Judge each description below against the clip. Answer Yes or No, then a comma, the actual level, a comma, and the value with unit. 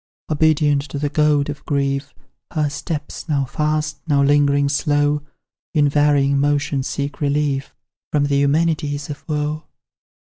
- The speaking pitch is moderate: Yes, medium, 145 Hz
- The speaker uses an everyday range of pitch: No, narrow, 1.1 semitones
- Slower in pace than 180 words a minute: Yes, slow, 135 wpm